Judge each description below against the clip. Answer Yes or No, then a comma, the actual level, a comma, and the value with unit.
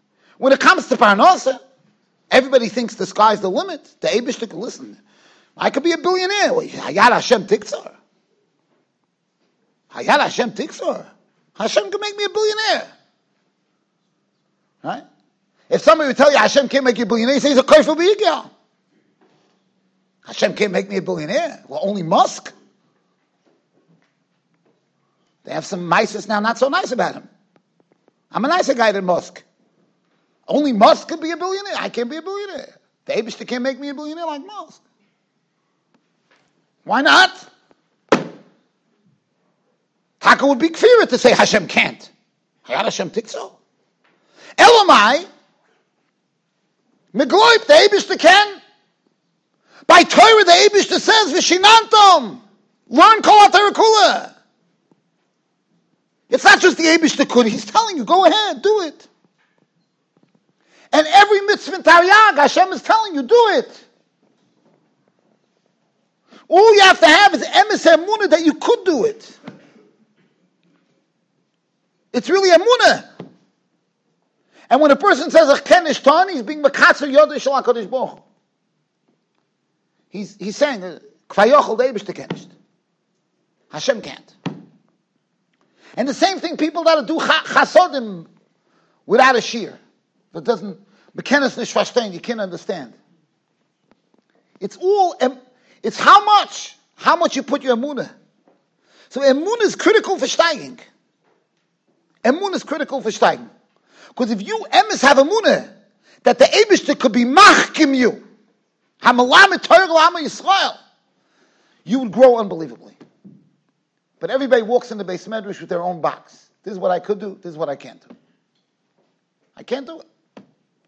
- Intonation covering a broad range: Yes, wide, 7.1 semitones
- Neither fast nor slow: No, slow, 130 wpm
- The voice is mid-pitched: No, very high, 300 Hz